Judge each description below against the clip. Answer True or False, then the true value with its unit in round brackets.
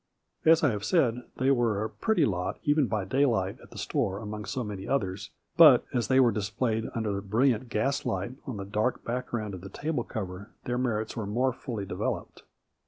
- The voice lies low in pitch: True (110 Hz)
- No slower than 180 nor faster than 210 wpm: True (195 wpm)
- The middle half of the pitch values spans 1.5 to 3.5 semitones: False (4.1 semitones)